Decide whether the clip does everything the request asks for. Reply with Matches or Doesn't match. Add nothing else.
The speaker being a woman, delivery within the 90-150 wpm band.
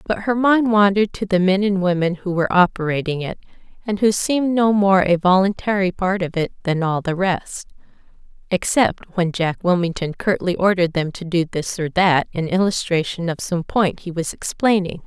Doesn't match